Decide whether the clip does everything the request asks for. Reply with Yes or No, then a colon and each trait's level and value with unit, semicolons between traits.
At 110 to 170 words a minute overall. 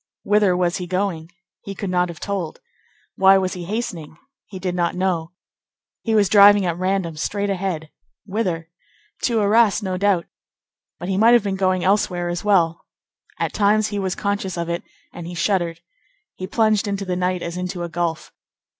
No: average, 180 wpm